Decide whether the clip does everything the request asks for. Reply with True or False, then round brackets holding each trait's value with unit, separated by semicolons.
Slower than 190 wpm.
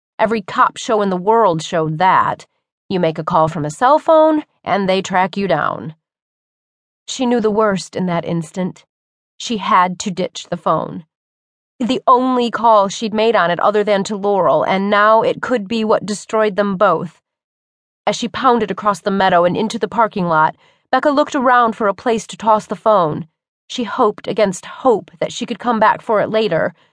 False (195 wpm)